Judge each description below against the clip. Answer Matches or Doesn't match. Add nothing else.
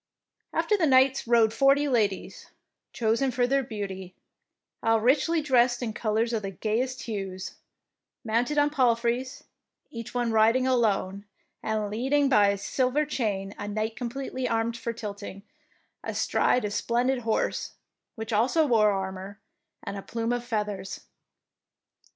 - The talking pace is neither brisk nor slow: Matches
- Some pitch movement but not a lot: Matches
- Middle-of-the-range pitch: Doesn't match